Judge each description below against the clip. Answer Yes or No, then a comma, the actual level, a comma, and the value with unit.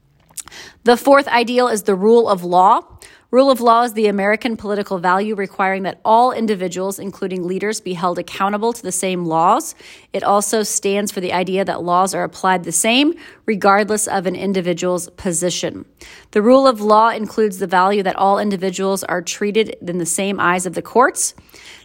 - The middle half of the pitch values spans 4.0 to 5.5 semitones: No, average, 3.3 semitones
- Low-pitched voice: No, high, 195 Hz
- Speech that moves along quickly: No, average, 180 wpm